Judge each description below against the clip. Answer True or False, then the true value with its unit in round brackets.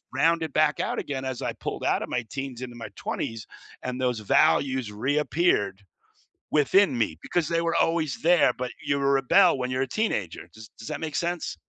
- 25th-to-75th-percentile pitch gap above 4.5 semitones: True (5.1 semitones)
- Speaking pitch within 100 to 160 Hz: True (135 Hz)